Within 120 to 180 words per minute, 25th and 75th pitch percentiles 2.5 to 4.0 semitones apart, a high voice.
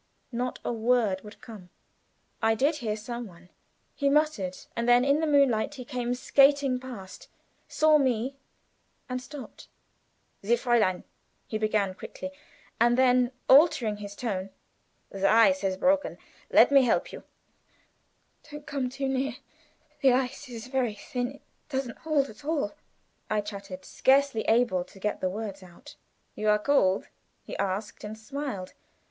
No: average, 150 wpm; average, 4.6 semitones; high, 240 Hz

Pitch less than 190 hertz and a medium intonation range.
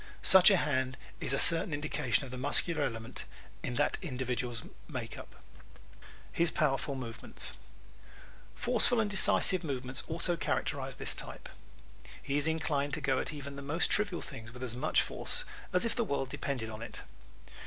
Yes: medium, 140 Hz; average, 4.7 semitones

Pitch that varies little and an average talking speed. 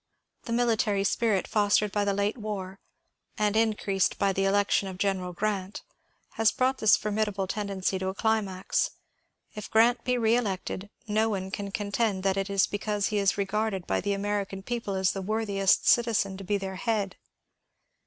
Yes: narrow, 1.9 semitones; average, 170 wpm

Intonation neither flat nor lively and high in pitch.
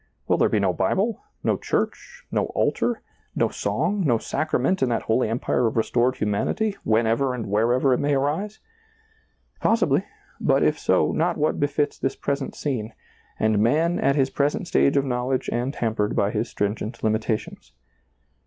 No: average, 4.7 semitones; low, 125 Hz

